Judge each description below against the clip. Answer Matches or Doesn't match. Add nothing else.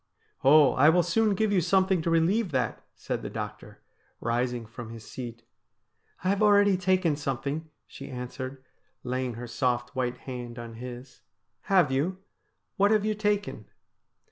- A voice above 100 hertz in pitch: Matches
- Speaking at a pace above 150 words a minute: Matches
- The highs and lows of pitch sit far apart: Matches